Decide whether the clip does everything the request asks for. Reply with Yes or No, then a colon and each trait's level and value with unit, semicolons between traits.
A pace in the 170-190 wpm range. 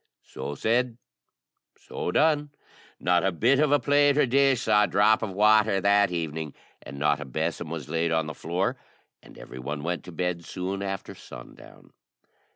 Yes: average, 175 wpm